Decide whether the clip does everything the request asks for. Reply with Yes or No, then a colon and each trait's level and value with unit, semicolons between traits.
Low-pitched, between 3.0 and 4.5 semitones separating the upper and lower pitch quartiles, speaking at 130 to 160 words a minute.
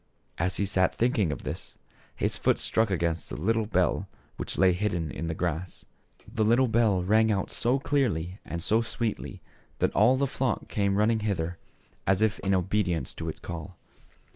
No: low, 100 Hz; average, 4.1 semitones; average, 175 wpm